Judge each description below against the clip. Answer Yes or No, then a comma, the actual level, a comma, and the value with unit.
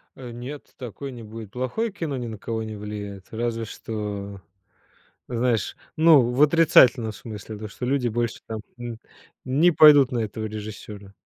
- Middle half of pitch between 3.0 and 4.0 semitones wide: Yes, average, 3.3 semitones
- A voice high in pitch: No, low, 115 Hz